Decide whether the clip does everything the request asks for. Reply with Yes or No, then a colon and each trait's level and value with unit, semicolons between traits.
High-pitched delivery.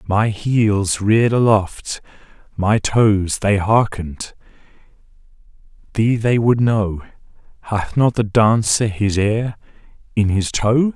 No: low, 105 Hz